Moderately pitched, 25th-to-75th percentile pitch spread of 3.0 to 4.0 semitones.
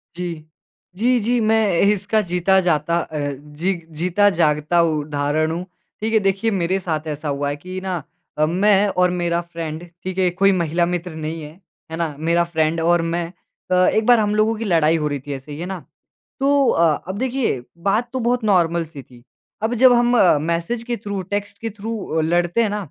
No: medium, 175 Hz; average, 4.5 semitones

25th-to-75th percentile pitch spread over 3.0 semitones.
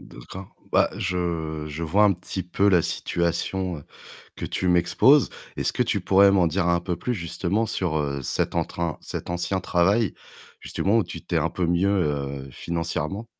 No: average, 2.7 semitones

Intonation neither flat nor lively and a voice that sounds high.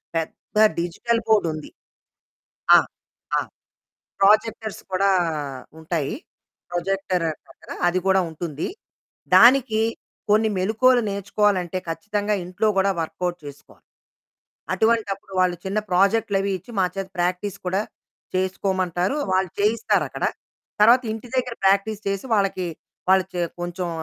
Yes: average, 3.0 semitones; high, 195 Hz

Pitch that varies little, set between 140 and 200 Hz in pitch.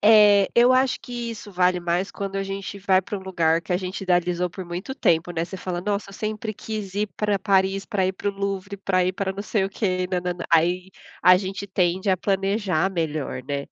Yes: narrow, 2.1 semitones; high, 190 Hz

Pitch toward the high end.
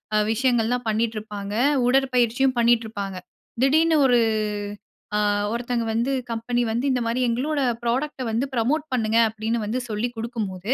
Yes: high, 235 Hz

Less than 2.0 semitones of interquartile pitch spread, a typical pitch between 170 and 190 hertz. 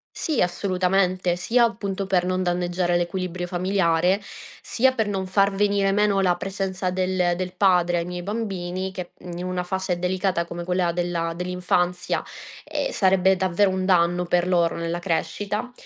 Yes: narrow, 1.6 semitones; medium, 185 Hz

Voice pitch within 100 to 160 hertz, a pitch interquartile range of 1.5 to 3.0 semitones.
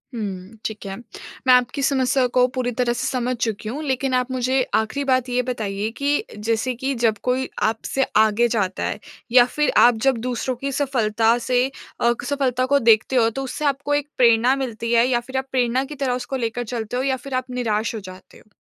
No: high, 245 Hz; average, 2.7 semitones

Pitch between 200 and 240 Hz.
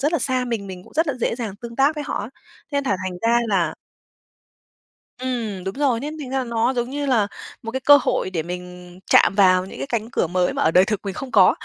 Yes: high, 230 Hz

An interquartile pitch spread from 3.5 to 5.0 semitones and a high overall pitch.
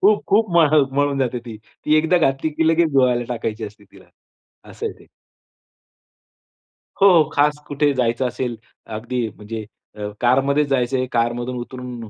No: average, 3.8 semitones; low, 130 Hz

